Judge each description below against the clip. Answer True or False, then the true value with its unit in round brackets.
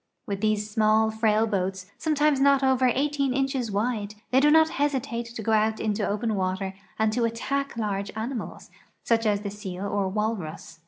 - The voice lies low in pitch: False (220 Hz)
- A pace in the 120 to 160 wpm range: False (175 wpm)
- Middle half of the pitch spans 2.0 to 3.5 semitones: False (4.2 semitones)